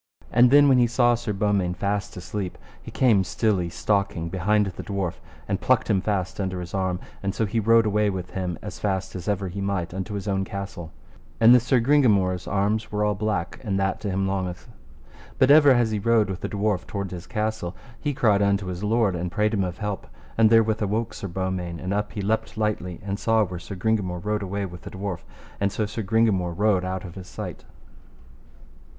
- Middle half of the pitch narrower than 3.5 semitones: Yes, narrow, 2.6 semitones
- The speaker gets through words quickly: Yes, fast, 215 wpm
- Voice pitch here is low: Yes, low, 100 Hz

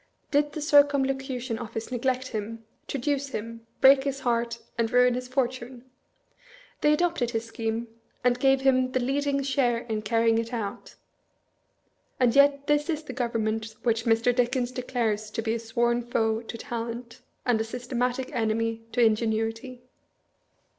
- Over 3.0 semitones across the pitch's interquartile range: No, average, 2.7 semitones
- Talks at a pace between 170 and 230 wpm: No, average, 150 wpm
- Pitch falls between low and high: No, high, 245 Hz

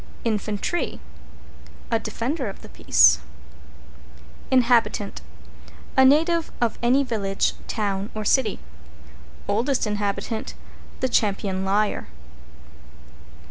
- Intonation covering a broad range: No, average, 4.1 semitones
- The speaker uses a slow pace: Yes, slow, 90 wpm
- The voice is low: No, high, 220 Hz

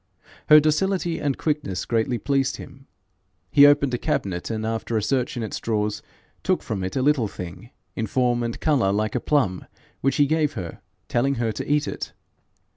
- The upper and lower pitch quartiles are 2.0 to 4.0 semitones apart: No, average, 5.0 semitones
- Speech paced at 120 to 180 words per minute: No, average, 190 wpm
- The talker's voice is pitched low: Yes, low, 120 Hz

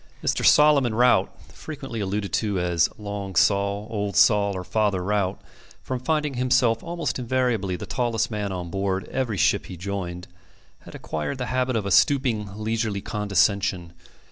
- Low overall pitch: Yes, low, 105 Hz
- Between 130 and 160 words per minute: Yes, average, 155 wpm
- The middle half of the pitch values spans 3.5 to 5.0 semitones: Yes, average, 4.2 semitones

